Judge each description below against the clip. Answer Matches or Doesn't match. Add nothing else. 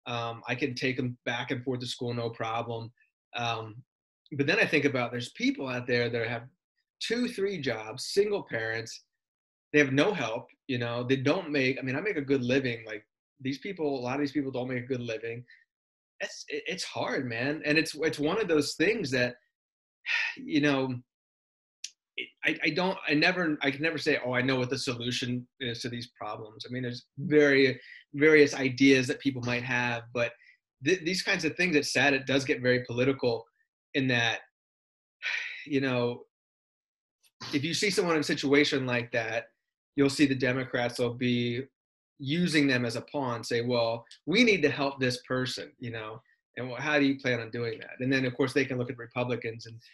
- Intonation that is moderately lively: Matches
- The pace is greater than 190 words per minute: Matches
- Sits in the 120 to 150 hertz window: Matches